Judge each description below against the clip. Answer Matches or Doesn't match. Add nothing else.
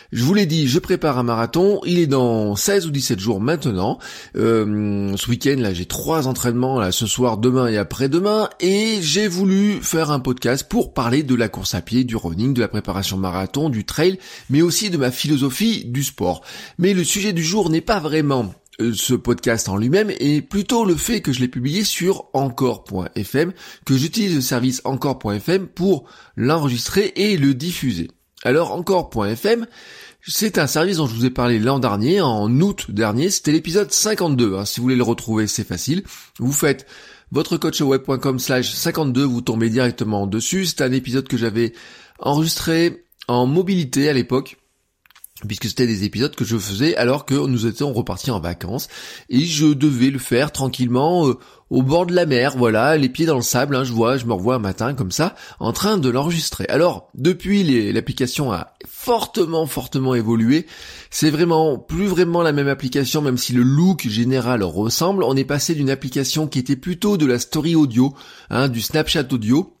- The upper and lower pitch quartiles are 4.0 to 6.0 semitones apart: Matches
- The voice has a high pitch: Doesn't match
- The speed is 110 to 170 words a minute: Doesn't match